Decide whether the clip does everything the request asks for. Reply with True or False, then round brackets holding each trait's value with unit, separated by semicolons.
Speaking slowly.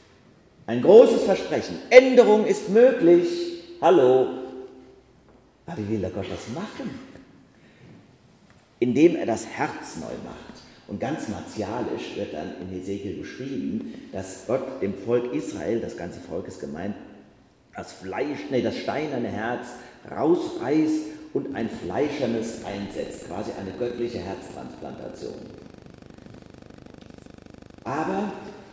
True (110 wpm)